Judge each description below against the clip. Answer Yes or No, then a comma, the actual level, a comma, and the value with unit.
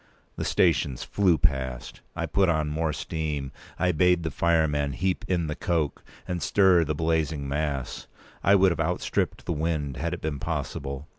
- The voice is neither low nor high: No, very low, 80 Hz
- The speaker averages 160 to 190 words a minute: Yes, average, 170 wpm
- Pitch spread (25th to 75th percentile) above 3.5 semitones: No, average, 3.0 semitones